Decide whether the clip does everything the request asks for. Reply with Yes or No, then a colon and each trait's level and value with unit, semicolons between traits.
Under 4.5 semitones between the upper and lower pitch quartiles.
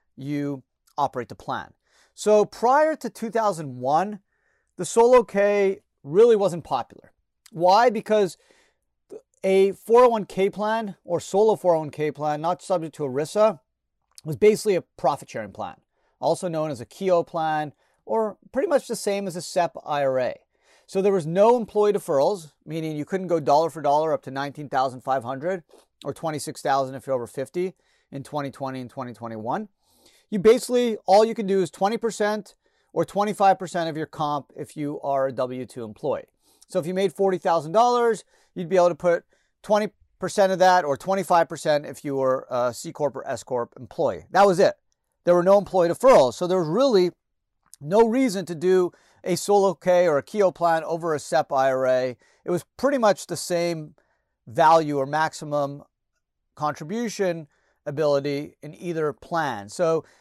No: wide, 5.6 semitones